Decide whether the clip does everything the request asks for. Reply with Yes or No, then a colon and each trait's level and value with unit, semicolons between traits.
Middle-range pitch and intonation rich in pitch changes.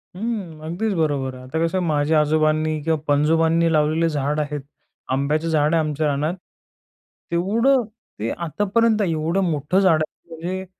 No: medium, 160 Hz; average, 2.7 semitones